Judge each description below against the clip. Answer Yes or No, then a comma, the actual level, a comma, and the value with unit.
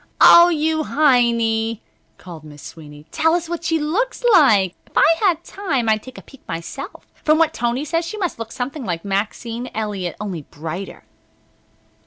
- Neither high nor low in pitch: No, high, 245 Hz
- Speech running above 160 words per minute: Yes, average, 170 wpm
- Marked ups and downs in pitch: Yes, wide, 8.2 semitones